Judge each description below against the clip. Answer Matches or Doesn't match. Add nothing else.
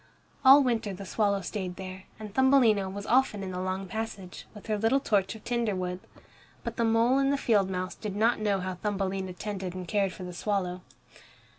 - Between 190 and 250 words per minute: Matches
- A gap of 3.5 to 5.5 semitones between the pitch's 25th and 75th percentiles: Doesn't match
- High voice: Matches